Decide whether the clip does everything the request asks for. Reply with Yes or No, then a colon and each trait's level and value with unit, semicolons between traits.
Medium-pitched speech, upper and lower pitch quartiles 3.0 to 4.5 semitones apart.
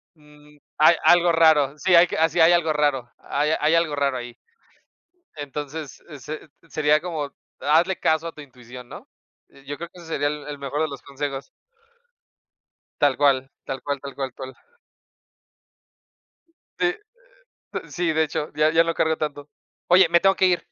No: medium, 150 Hz; narrow, 2.5 semitones